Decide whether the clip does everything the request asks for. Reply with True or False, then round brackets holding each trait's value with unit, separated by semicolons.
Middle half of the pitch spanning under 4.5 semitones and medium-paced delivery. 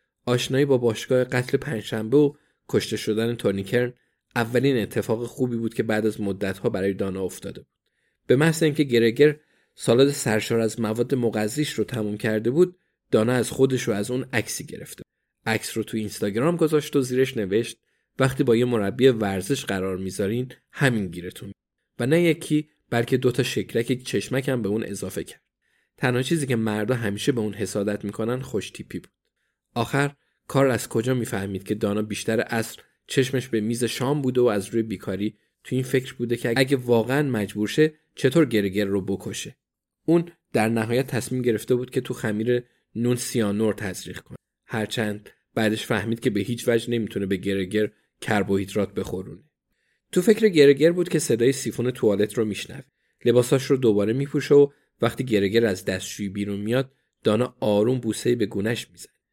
False (3.8 semitones; 165 wpm)